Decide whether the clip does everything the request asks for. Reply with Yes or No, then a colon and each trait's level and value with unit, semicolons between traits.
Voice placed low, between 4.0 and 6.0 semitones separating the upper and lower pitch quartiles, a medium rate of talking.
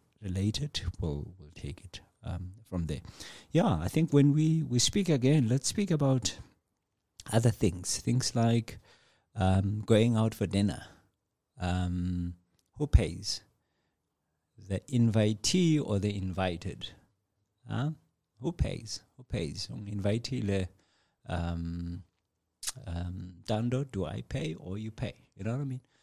No: low, 105 Hz; wide, 5.4 semitones; slow, 130 wpm